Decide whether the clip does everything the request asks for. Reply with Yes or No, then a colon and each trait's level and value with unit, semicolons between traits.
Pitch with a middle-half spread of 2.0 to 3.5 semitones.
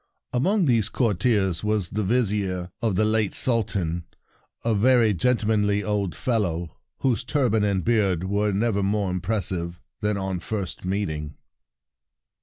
Yes: average, 3.2 semitones